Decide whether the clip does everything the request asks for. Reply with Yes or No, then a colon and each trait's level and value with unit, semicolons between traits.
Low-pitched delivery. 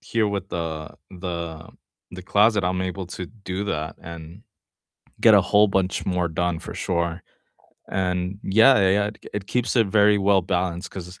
Yes: very low, 95 Hz